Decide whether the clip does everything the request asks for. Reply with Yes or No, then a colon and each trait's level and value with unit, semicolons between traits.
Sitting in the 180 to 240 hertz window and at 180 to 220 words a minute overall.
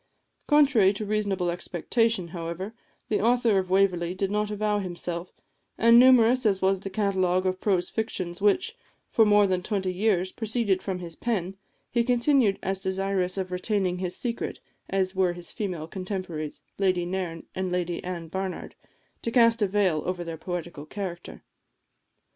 No: high, 190 Hz; average, 160 wpm